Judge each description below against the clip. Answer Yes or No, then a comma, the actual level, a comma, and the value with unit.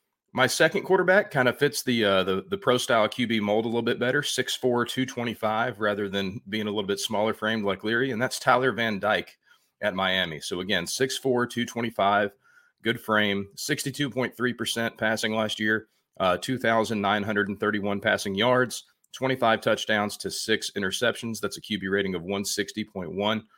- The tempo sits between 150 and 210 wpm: Yes, average, 160 wpm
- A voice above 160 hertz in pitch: No, low, 110 Hz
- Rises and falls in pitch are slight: No, average, 3.2 semitones